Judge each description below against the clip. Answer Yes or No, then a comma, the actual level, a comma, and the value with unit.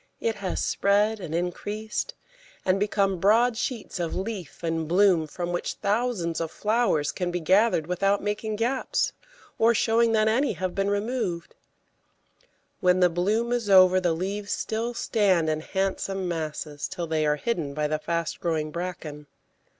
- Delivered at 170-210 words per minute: No, average, 160 wpm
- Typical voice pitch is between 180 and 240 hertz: Yes, high, 190 Hz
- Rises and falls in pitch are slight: No, average, 4.4 semitones